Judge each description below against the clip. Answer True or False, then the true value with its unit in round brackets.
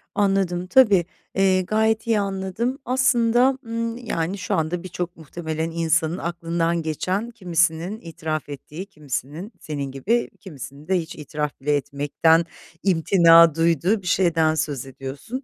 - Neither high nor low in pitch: True (170 Hz)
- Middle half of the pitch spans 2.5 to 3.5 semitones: False (4.0 semitones)